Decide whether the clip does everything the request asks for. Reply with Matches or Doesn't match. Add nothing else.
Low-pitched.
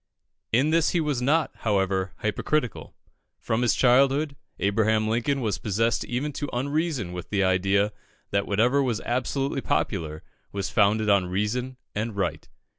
Matches